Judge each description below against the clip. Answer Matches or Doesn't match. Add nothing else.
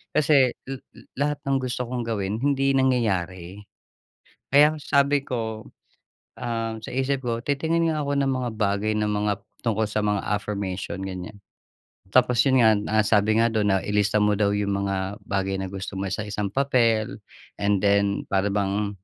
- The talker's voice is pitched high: Doesn't match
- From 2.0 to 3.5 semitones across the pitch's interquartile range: Doesn't match